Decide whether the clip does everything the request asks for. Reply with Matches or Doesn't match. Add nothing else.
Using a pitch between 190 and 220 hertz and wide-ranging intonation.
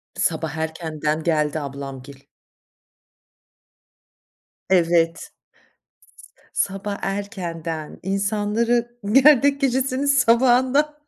Matches